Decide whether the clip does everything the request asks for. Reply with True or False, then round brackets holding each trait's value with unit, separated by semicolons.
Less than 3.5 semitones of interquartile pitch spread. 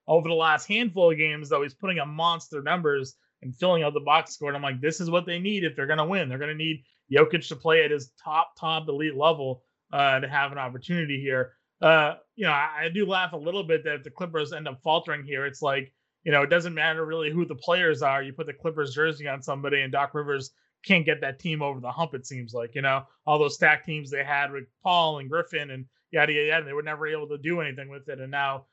True (2.8 semitones)